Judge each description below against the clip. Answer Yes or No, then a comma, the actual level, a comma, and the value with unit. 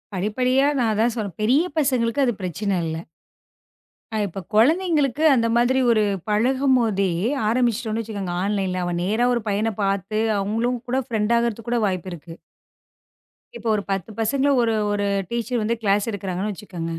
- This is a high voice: Yes, high, 220 Hz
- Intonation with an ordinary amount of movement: Yes, average, 3.4 semitones